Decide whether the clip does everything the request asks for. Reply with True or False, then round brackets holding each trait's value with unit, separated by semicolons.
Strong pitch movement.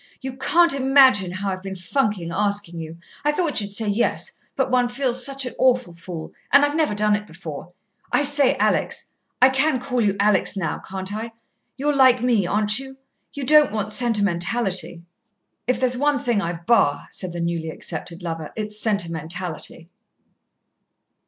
True (6.4 semitones)